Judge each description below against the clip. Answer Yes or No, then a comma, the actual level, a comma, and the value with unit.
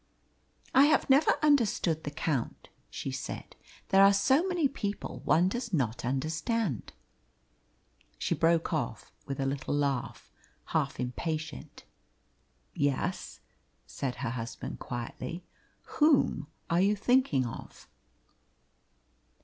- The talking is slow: Yes, slow, 110 wpm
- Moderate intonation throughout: No, wide, 8.2 semitones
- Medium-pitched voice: Yes, medium, 160 Hz